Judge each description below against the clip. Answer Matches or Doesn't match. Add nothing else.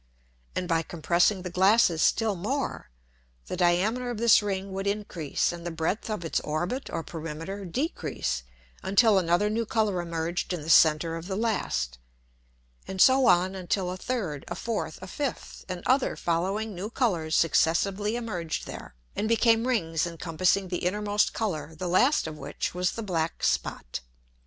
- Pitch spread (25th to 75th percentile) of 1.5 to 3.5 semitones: Doesn't match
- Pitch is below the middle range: Doesn't match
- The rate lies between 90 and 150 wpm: Doesn't match